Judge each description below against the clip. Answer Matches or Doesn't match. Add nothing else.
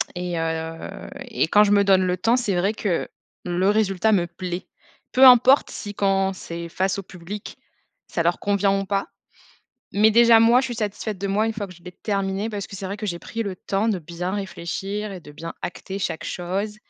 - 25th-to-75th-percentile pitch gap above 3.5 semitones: Doesn't match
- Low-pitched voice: Doesn't match